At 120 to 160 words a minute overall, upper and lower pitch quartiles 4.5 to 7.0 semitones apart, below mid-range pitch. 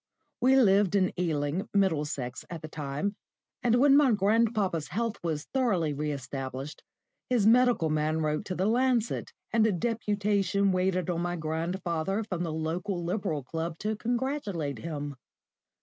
No: average, 150 wpm; wide, 5.5 semitones; medium, 185 Hz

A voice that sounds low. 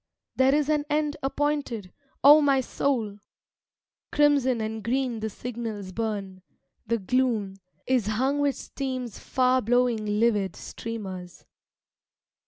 No: high, 240 Hz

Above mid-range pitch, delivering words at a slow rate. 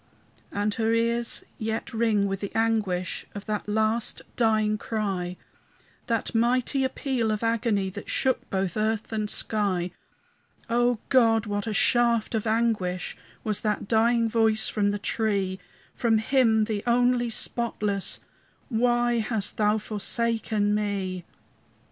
Yes: high, 220 Hz; slow, 130 wpm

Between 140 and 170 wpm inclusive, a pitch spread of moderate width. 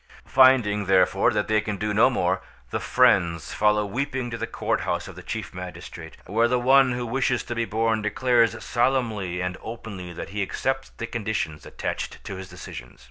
No: average, 185 wpm; average, 4.2 semitones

